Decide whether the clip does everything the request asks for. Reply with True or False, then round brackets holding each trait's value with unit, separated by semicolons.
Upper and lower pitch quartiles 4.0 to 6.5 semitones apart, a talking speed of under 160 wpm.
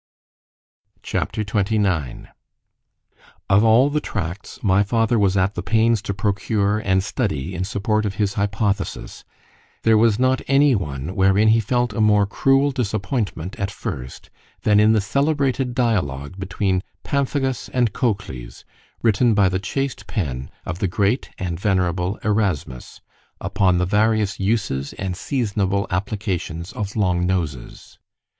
False (3.3 semitones; 145 wpm)